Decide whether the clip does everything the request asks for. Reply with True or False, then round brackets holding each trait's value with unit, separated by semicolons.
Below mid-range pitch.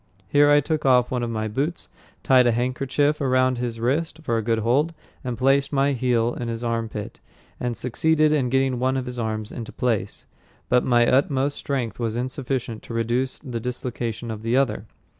True (125 Hz)